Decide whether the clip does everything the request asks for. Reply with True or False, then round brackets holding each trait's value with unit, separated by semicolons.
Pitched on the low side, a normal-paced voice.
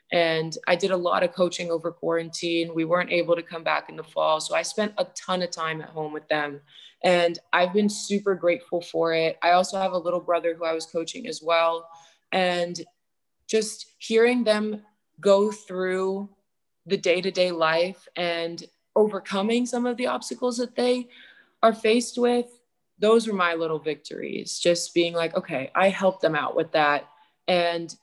False (175 Hz; 185 wpm)